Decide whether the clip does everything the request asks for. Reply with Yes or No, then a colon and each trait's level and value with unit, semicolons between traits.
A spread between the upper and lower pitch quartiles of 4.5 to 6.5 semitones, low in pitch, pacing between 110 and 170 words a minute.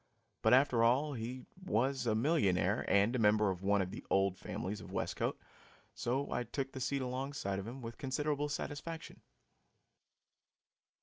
Yes: average, 5.0 semitones; low, 120 Hz; average, 160 wpm